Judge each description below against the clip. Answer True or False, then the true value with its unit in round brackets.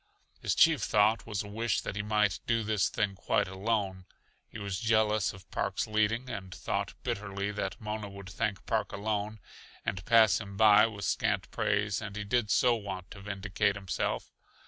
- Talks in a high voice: False (105 Hz)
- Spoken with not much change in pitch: True (1.7 semitones)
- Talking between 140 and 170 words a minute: False (180 wpm)